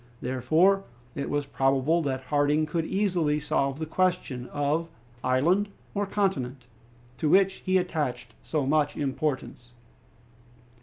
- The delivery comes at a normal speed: No, slow, 120 wpm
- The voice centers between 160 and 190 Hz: No, medium, 150 Hz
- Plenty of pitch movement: No, average, 4.7 semitones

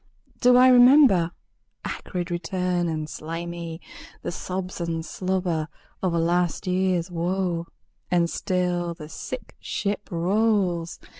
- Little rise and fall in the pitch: Yes, narrow, 2.0 semitones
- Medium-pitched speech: Yes, medium, 175 Hz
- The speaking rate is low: Yes, slow, 120 wpm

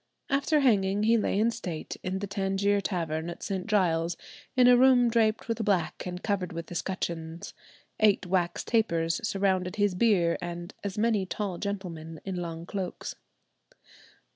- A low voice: No, high, 195 Hz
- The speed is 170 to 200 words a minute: No, average, 155 wpm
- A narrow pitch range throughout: No, average, 3.6 semitones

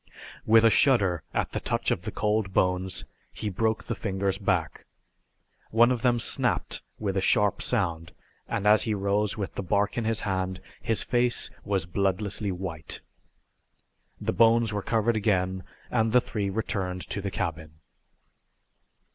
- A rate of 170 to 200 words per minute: No, average, 155 wpm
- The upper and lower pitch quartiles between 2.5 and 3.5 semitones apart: Yes, average, 3.0 semitones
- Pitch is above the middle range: No, low, 100 Hz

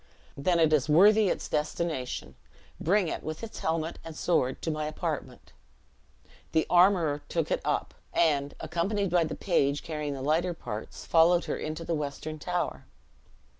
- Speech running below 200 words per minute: Yes, average, 160 wpm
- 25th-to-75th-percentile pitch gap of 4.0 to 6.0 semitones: No, narrow, 2.6 semitones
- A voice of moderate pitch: Yes, medium, 160 Hz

